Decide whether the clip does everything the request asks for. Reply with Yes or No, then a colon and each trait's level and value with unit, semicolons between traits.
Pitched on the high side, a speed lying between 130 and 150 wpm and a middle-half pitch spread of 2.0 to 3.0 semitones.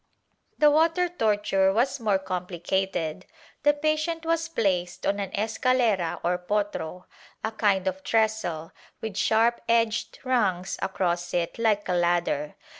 No: high, 205 Hz; average, 140 wpm; average, 4.5 semitones